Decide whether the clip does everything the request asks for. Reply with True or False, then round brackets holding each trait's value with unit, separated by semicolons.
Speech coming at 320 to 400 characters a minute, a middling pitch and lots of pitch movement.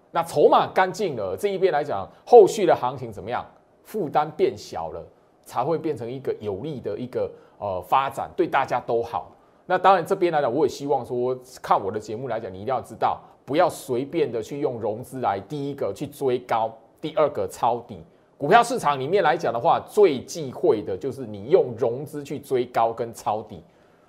False (285 characters per minute; 150 Hz; 8.2 semitones)